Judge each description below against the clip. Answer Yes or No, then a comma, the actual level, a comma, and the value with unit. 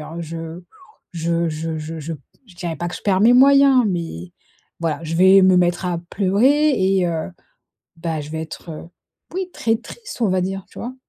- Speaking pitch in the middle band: Yes, medium, 175 Hz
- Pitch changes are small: No, average, 3.7 semitones